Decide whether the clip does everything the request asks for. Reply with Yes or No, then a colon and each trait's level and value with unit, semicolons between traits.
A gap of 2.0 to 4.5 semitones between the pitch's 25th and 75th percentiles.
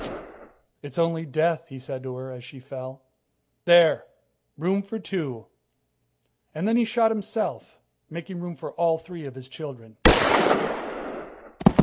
No: average, 5.0 semitones